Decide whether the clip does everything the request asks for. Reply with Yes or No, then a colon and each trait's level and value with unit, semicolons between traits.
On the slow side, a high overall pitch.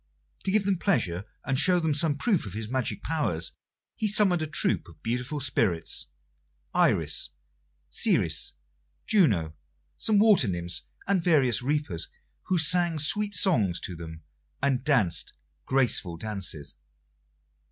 No: slow, 130 wpm; low, 135 Hz